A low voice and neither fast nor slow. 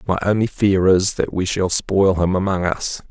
No: very low, 95 Hz; fast, 215 wpm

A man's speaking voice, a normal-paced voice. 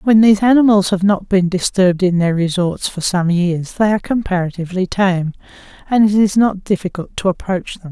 No: female; average, 190 wpm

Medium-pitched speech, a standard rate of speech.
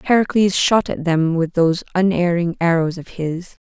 Yes: medium, 175 Hz; average, 165 wpm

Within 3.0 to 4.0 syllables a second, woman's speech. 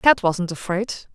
Yes: 3.8 syllables/s; female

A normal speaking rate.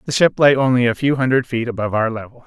No: fast, 270 wpm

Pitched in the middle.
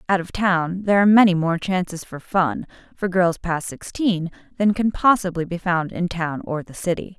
Yes: medium, 180 Hz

